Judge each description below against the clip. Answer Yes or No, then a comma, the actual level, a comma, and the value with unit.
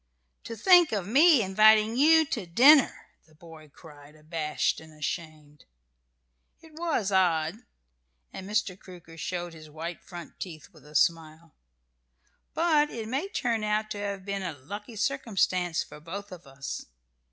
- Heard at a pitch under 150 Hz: No, medium, 185 Hz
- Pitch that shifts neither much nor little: No, wide, 5.8 semitones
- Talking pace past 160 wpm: No, average, 150 wpm